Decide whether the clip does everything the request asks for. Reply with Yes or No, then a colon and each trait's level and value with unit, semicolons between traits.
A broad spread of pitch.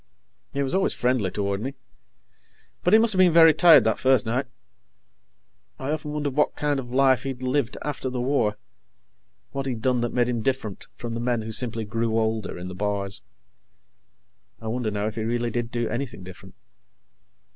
No: average, 3.6 semitones